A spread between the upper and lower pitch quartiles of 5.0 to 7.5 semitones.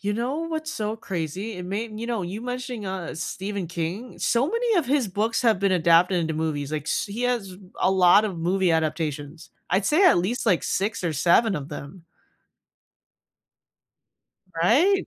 Yes: wide, 5.4 semitones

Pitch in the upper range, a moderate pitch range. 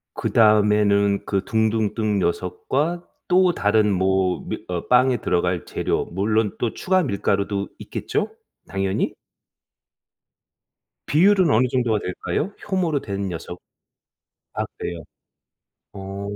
No: low, 105 Hz; average, 4.7 semitones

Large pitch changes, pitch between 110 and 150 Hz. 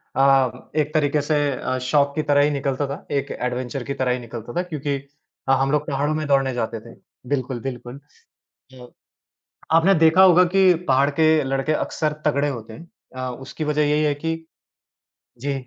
No: average, 2.8 semitones; medium, 140 Hz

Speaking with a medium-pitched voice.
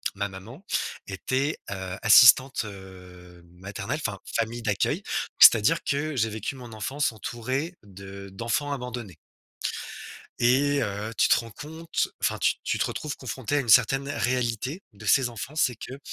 No: low, 115 Hz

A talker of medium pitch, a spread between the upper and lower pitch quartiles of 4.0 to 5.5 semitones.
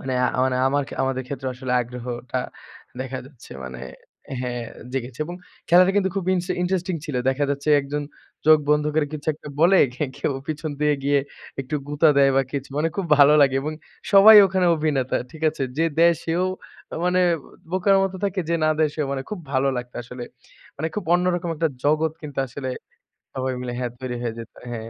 Yes: medium, 145 Hz; average, 4.5 semitones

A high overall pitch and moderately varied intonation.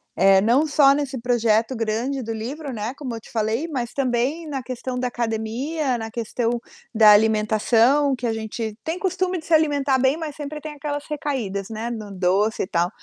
Yes: high, 245 Hz; average, 4.6 semitones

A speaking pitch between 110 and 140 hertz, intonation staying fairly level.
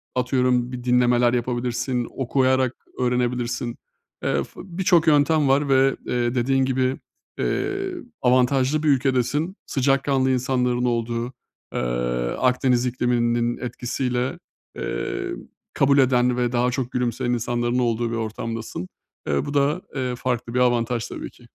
Yes: low, 125 Hz; narrow, 1.7 semitones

